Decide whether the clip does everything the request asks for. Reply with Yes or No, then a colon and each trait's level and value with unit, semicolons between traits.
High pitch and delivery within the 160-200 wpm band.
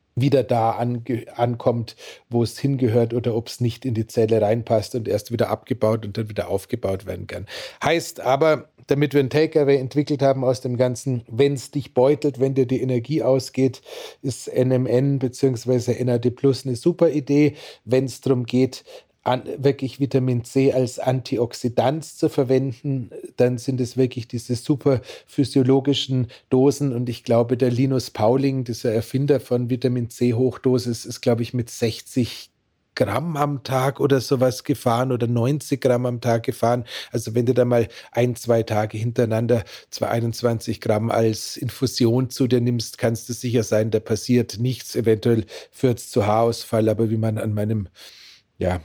No: low, 125 Hz; average, 170 wpm